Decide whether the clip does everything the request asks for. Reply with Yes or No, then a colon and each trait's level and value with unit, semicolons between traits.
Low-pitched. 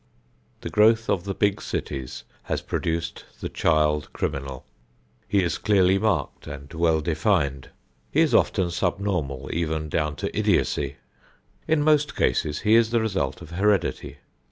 Yes: very low, 85 Hz